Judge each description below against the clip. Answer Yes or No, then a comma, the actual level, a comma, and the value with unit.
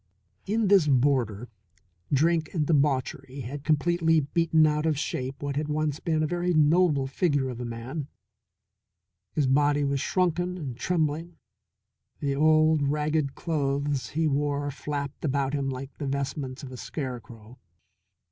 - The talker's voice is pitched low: No, medium, 145 Hz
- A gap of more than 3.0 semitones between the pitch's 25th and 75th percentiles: No, narrow, 2.5 semitones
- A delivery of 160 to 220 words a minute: No, average, 145 wpm